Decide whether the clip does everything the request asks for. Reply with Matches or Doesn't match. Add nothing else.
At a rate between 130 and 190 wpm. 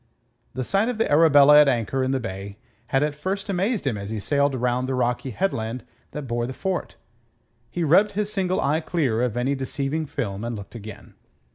Doesn't match